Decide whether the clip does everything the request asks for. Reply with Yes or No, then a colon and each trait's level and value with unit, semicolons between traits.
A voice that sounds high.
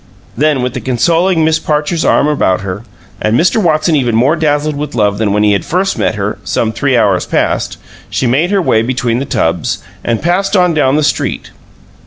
No: medium, 140 Hz